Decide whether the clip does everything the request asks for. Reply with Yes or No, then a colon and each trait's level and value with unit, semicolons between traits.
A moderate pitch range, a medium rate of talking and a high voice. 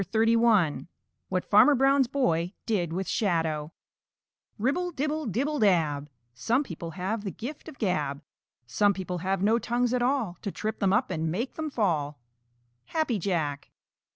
No: wide, 6.7 semitones; average, 155 wpm; high, 205 Hz